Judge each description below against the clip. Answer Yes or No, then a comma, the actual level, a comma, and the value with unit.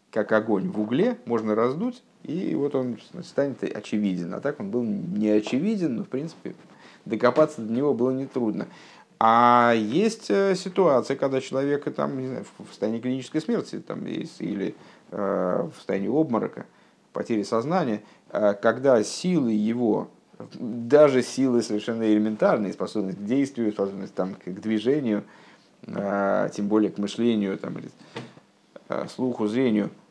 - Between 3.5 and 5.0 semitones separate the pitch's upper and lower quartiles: Yes, average, 4.6 semitones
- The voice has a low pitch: Yes, low, 120 Hz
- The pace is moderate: Yes, average, 130 wpm